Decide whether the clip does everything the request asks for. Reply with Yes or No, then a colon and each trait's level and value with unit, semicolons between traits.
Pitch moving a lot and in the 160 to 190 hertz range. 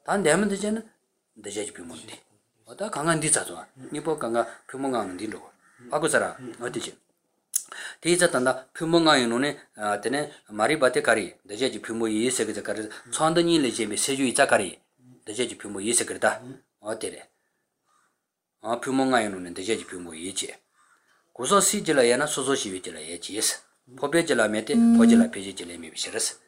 No: wide, 6.6 semitones; medium, 140 Hz